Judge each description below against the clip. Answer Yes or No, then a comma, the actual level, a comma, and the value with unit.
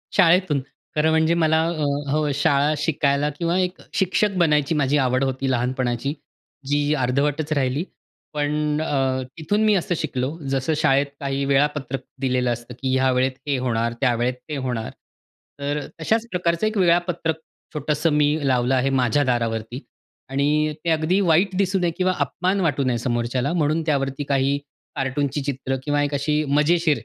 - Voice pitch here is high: No, medium, 145 Hz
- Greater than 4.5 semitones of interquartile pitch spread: No, average, 3.3 semitones